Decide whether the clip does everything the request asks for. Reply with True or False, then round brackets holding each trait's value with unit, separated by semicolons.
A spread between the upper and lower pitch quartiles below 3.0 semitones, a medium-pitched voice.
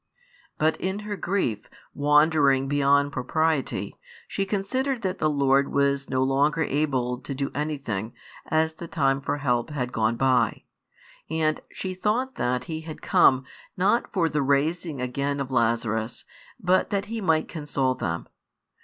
False (3.7 semitones; 145 Hz)